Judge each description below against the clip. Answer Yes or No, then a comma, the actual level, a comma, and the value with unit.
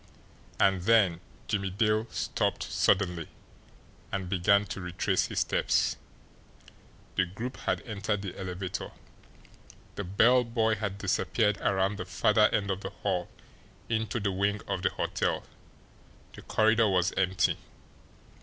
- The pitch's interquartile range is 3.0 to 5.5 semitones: No, narrow, 2.5 semitones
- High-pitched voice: No, low, 100 Hz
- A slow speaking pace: Yes, slow, 130 wpm